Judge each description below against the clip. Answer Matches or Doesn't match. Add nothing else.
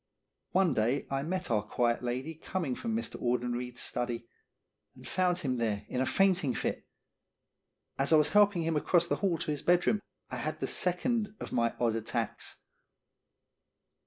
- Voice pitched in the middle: Matches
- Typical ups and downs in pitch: Doesn't match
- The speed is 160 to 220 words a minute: Matches